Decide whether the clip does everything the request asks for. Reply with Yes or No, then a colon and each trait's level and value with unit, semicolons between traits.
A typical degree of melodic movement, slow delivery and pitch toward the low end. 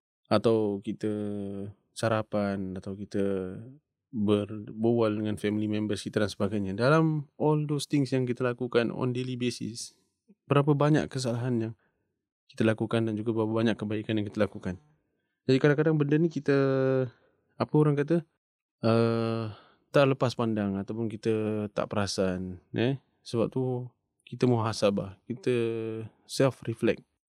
Yes: average, 3.8 semitones; slow, 130 wpm; low, 115 Hz